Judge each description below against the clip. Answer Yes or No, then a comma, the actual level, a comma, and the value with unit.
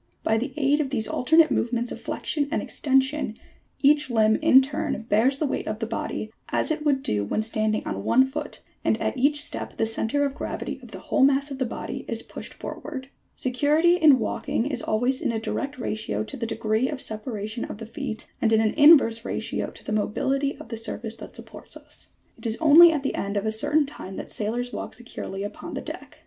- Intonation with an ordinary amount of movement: Yes, average, 4.6 semitones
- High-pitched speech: Yes, very high, 255 Hz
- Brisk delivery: Yes, fast, 220 wpm